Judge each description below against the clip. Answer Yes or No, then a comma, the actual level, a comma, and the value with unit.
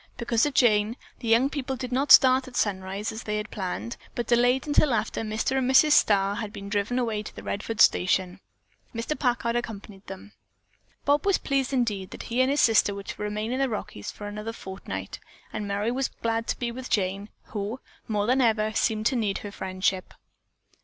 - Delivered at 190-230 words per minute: Yes, average, 200 wpm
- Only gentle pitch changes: No, average, 3.4 semitones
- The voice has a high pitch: Yes, high, 225 Hz